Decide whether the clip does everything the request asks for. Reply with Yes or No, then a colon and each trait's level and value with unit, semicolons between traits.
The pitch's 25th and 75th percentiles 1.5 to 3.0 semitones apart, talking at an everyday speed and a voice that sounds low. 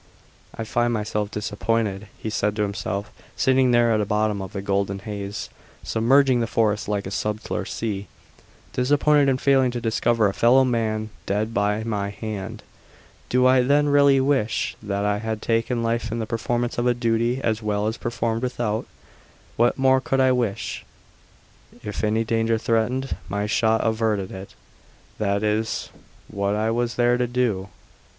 Yes: narrow, 2.6 semitones; average, 165 wpm; low, 115 Hz